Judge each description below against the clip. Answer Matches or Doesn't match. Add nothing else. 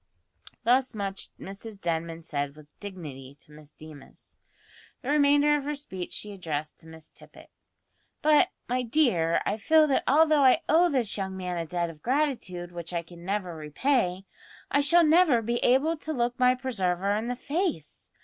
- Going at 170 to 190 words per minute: Matches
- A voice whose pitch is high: Matches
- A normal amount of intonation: Doesn't match